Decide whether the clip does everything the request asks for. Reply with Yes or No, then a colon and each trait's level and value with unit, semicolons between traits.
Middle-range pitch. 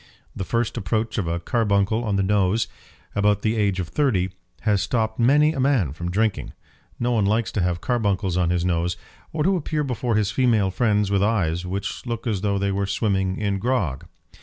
No: low, 105 Hz